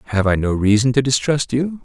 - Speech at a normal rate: No, fast, 230 wpm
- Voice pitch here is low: Yes, low, 125 Hz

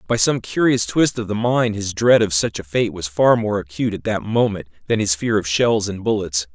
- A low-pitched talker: Yes, low, 105 Hz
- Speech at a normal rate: No, fast, 250 wpm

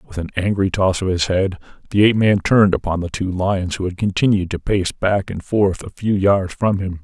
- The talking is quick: Yes, fast, 240 wpm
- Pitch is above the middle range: No, very low, 95 Hz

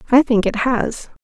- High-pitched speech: Yes, high, 235 Hz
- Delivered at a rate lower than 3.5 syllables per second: No, 4.5 syllables/s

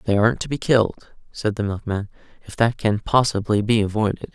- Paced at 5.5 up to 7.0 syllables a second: Yes, 5.7 syllables/s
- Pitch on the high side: No, low, 110 Hz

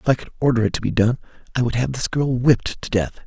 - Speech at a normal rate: No, fast, 295 wpm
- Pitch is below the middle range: Yes, low, 125 Hz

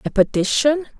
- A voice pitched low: No, very high, 250 Hz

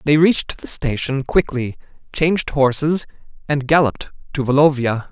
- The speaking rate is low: Yes, slow, 130 wpm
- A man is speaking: Yes, male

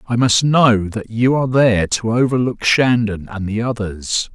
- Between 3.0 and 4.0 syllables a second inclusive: No, 4.6 syllables/s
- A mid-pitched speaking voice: No, low, 115 Hz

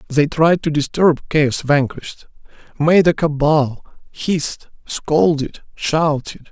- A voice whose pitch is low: No, medium, 150 Hz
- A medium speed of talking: No, slow, 110 wpm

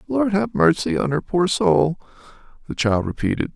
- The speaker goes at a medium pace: Yes, average, 170 wpm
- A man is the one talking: Yes, male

